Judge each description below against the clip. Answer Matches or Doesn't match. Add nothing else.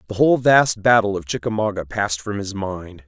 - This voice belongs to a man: Matches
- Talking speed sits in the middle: Matches